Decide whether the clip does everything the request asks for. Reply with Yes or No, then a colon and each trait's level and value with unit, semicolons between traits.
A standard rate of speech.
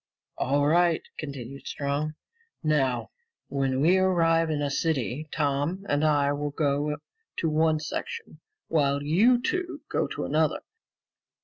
No: slow, 130 wpm